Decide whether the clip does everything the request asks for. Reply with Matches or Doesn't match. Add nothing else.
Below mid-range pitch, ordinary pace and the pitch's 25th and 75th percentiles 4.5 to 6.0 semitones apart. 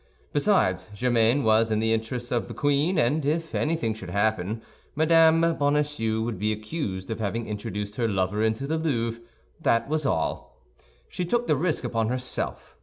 Matches